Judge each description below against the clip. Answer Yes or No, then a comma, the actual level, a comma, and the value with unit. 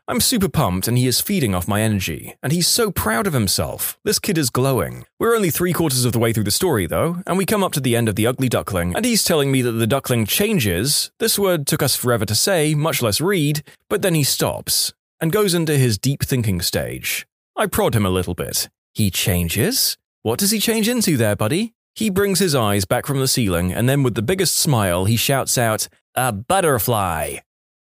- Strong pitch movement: Yes, wide, 8.2 semitones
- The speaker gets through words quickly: Yes, fast, 225 wpm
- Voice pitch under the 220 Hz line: Yes, low, 135 Hz